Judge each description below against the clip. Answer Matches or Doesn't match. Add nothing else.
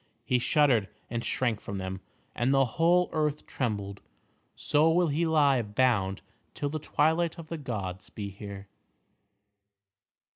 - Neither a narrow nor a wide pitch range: Doesn't match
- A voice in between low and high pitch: Doesn't match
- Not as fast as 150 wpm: Matches